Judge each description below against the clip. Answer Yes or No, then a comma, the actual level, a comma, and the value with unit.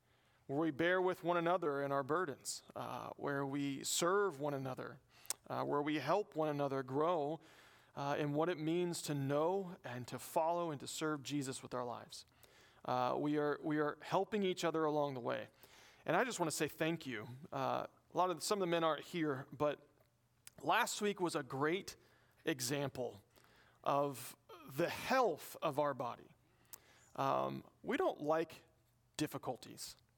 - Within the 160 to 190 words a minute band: Yes, average, 170 wpm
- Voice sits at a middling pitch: Yes, medium, 150 Hz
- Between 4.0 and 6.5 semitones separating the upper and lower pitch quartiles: No, average, 3.6 semitones